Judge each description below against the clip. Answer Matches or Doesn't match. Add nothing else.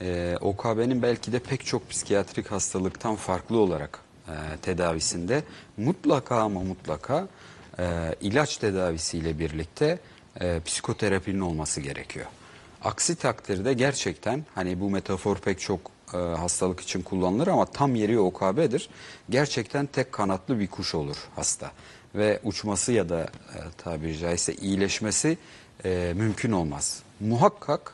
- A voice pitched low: Matches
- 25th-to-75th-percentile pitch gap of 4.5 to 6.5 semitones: Matches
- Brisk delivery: Doesn't match